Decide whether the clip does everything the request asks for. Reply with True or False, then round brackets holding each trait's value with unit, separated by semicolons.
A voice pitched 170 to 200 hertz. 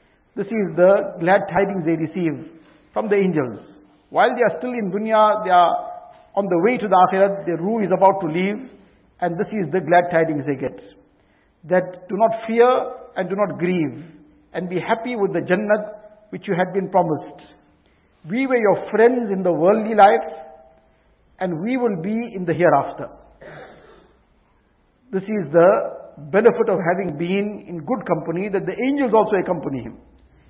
True (190 Hz)